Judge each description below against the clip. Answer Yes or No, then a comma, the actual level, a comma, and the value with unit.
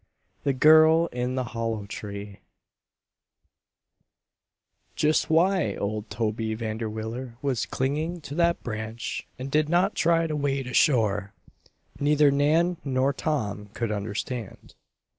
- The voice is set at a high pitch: No, low, 130 Hz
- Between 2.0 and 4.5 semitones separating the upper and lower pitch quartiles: No, wide, 5.6 semitones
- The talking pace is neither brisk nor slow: No, slow, 115 wpm